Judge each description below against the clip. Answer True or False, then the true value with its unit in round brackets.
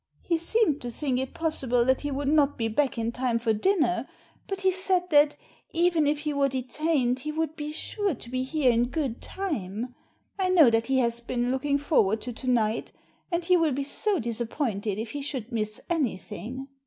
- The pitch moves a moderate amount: True (4.8 semitones)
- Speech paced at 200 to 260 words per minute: True (205 wpm)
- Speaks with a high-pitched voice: True (270 Hz)